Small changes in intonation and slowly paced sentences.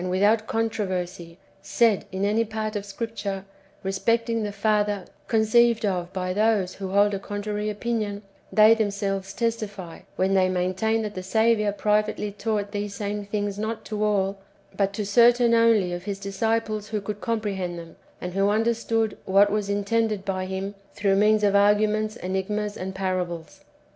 No: narrow, 2.0 semitones; average, 160 wpm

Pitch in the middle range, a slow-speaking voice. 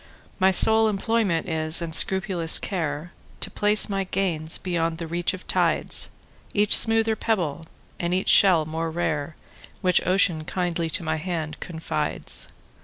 Yes: medium, 175 Hz; slow, 130 wpm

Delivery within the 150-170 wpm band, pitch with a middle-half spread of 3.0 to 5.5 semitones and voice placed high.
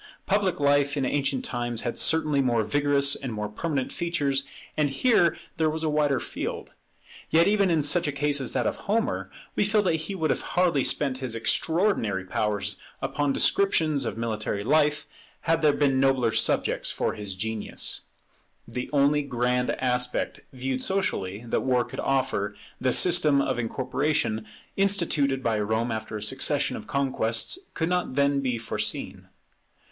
No: average, 160 wpm; average, 4.4 semitones; medium, 140 Hz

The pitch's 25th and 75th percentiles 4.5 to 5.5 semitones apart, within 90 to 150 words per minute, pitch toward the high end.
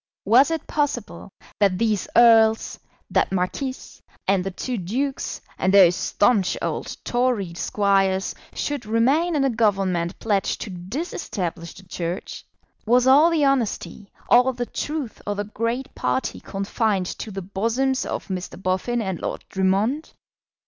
Yes: average, 5.0 semitones; average, 140 wpm; high, 215 Hz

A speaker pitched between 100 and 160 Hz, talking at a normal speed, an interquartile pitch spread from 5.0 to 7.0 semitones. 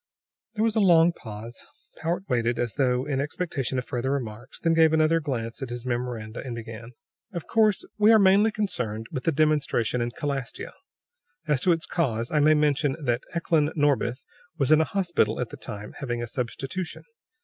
Yes: medium, 140 Hz; average, 185 wpm; wide, 5.4 semitones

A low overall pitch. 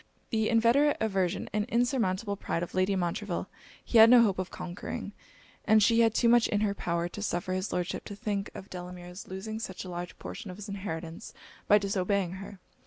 No: high, 200 Hz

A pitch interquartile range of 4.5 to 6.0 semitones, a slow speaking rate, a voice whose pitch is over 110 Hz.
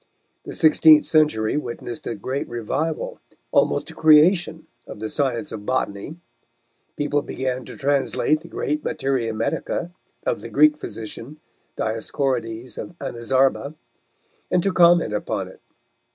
Yes: average, 5.0 semitones; slow, 130 wpm; medium, 140 Hz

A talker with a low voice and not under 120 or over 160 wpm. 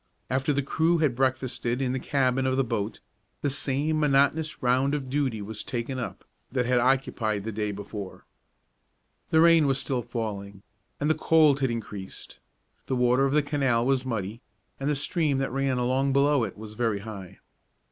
No: low, 130 Hz; average, 175 wpm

